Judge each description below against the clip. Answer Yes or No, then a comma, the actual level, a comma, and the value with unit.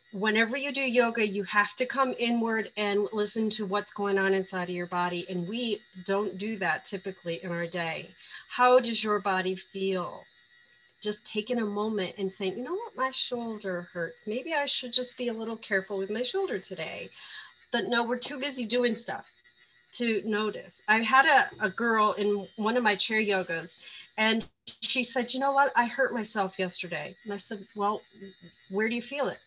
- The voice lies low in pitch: No, high, 210 Hz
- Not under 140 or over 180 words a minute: No, average, 195 wpm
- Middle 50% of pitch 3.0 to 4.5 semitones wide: Yes, average, 3.8 semitones